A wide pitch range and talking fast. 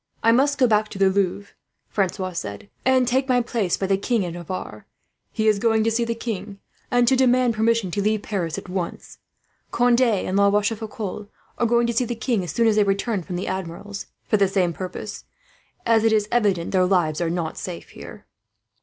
No: average, 3.7 semitones; fast, 210 wpm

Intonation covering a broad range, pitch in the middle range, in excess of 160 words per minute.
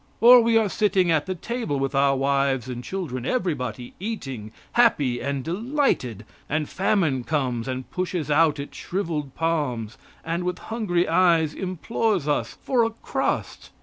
No: wide, 6.2 semitones; medium, 160 Hz; average, 150 wpm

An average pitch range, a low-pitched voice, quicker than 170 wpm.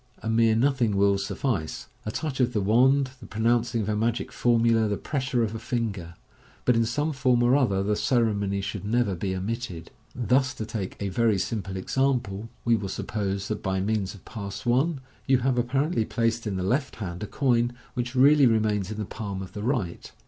Yes: average, 3.7 semitones; low, 115 Hz; fast, 205 wpm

